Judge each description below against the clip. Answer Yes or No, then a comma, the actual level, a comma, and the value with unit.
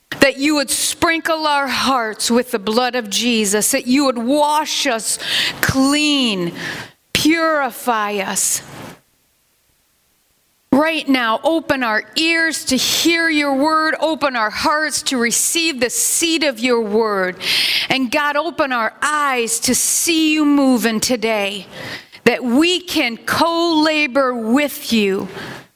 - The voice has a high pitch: Yes, very high, 275 Hz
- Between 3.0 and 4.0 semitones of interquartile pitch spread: No, average, 4.6 semitones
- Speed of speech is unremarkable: No, slow, 130 wpm